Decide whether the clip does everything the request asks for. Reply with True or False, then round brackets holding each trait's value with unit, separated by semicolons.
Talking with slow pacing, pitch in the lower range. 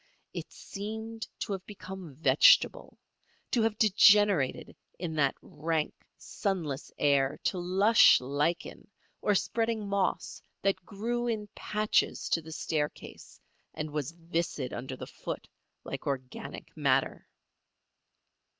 False (115 wpm; 185 Hz)